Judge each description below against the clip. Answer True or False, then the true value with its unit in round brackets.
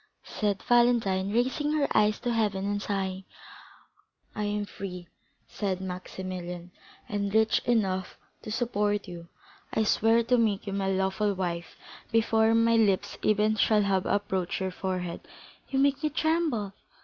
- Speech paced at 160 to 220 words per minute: False (145 wpm)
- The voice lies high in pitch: True (205 Hz)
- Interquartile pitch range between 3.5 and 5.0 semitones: False (3.1 semitones)